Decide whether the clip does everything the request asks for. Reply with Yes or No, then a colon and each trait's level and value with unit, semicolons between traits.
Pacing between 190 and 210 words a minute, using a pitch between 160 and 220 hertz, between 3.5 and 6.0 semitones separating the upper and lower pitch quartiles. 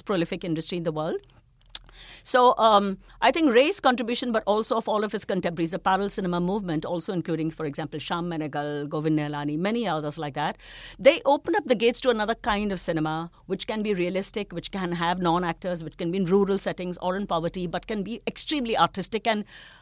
Yes: fast, 205 wpm; medium, 185 Hz; average, 4.6 semitones